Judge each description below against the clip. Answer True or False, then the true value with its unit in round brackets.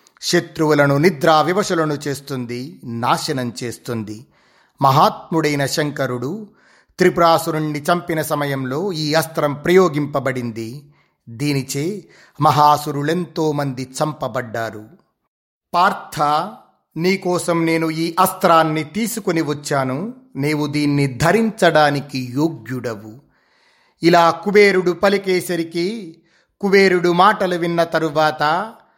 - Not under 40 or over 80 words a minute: True (75 wpm)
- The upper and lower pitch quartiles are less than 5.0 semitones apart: True (3.9 semitones)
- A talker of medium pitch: True (155 Hz)